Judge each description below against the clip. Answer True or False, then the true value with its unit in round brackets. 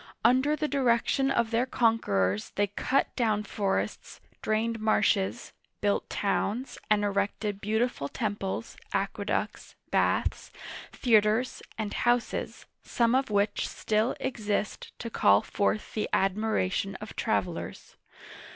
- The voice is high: True (215 Hz)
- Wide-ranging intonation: False (2.8 semitones)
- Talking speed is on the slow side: True (115 wpm)